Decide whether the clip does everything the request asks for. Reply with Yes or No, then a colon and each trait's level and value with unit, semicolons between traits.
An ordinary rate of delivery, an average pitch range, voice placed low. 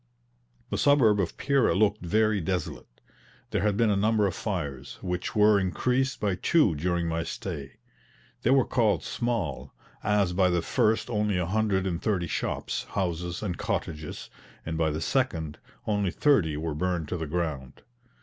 Yes: average, 165 wpm; average, 4.5 semitones; very low, 95 Hz